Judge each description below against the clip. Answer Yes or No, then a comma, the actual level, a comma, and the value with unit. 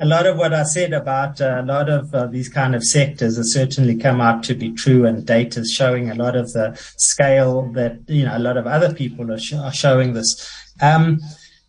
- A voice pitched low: Yes, low, 130 Hz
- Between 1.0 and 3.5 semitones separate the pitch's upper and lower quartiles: Yes, average, 3.2 semitones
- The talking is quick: Yes, fast, 230 wpm